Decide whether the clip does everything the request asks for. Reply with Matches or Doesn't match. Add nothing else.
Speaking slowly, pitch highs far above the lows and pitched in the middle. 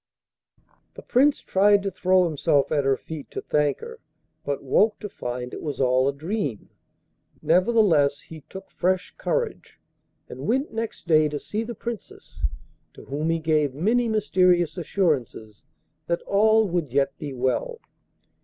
Doesn't match